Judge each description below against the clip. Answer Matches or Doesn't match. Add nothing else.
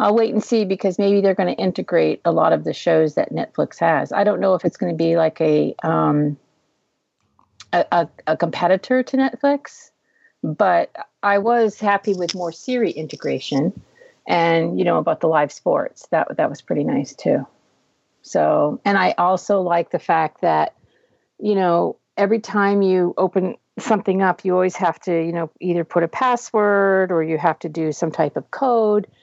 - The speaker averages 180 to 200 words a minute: Matches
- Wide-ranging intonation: Doesn't match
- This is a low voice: Doesn't match